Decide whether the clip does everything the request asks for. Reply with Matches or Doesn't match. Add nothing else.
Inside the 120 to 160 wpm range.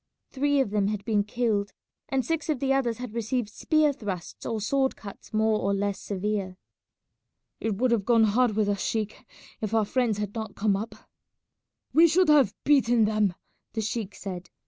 Doesn't match